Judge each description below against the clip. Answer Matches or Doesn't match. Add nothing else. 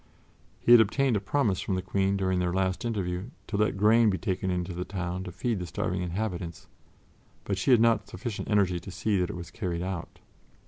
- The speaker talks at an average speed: Doesn't match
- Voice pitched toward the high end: Doesn't match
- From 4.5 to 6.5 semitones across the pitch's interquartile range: Doesn't match